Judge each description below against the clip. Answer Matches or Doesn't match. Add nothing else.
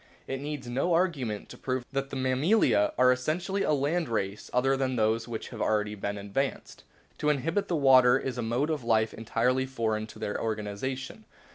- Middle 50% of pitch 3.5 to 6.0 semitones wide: Matches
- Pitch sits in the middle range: Doesn't match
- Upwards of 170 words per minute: Matches